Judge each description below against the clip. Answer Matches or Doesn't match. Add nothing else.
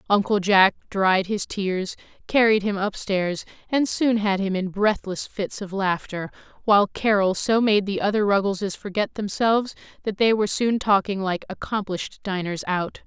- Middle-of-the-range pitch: Doesn't match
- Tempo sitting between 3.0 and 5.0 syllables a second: Matches